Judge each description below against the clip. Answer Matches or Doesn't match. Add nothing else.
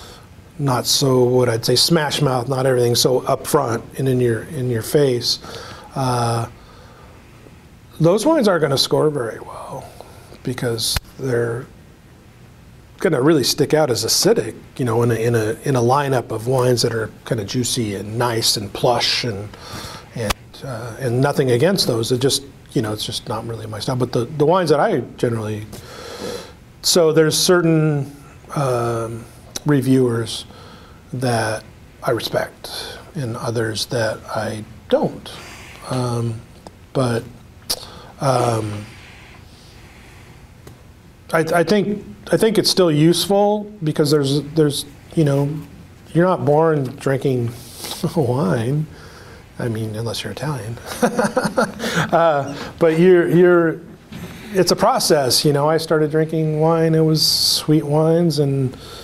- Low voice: Matches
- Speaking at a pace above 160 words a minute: Doesn't match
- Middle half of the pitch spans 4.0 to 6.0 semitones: Matches